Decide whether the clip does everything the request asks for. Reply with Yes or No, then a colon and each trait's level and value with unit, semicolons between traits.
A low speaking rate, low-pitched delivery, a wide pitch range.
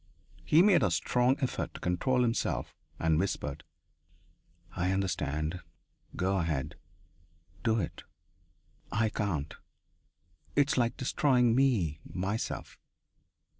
Yes: slow, 105 wpm; low, 100 Hz; wide, 6.9 semitones